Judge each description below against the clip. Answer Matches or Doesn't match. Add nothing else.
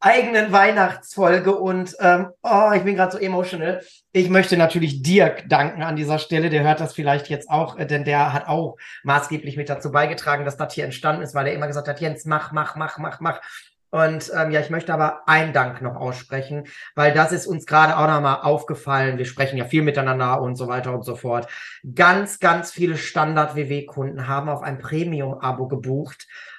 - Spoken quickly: Matches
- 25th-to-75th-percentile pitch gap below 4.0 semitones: Matches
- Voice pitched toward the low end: Doesn't match